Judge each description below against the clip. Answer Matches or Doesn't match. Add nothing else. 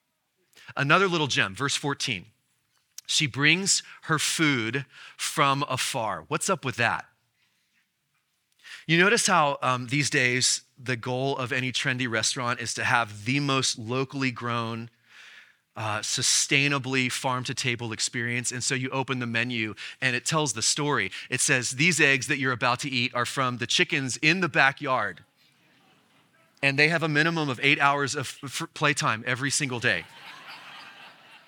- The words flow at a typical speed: Matches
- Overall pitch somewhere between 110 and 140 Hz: Matches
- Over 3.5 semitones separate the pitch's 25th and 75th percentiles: Doesn't match